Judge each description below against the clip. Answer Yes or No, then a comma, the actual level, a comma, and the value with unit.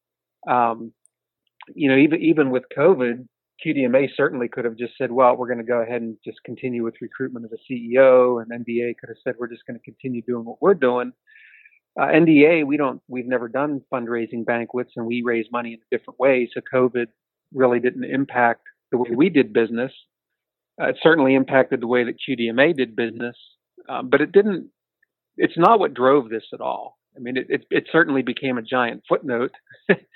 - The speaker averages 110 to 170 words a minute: No, average, 195 wpm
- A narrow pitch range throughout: Yes, narrow, 2.0 semitones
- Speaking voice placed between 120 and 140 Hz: Yes, low, 125 Hz